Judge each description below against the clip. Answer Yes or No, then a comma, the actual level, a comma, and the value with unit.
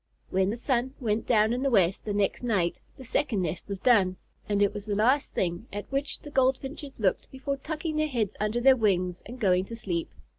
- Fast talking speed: Yes, fast, 220 wpm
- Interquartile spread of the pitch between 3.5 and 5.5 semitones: Yes, average, 5.1 semitones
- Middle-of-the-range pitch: No, high, 225 Hz